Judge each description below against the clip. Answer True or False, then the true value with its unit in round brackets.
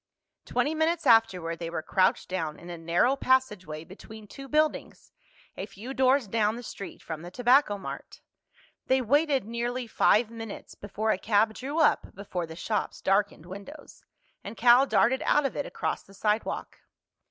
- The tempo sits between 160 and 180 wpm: True (165 wpm)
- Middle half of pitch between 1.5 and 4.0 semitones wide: False (5.5 semitones)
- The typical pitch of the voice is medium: False (220 Hz)